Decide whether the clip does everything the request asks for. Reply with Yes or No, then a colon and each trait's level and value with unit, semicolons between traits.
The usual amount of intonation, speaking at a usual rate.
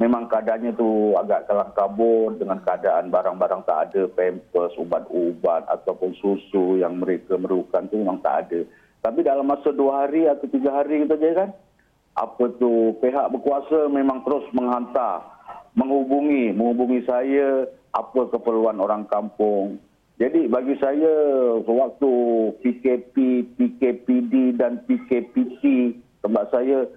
Yes: average, 4.0 semitones; average, 125 wpm